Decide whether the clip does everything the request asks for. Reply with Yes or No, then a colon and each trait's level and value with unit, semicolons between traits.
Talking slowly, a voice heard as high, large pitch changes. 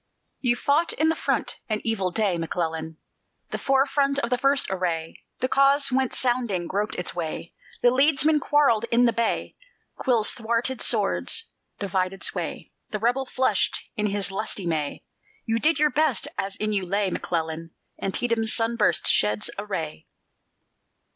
No: average, 155 wpm; high, 225 Hz; wide, 6.1 semitones